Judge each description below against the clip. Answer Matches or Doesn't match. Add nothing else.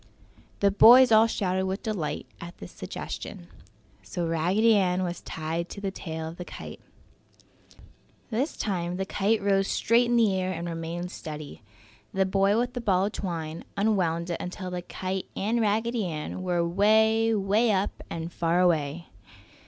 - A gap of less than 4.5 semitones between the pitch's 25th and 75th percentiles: Matches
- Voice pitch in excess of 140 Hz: Matches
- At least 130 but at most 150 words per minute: Doesn't match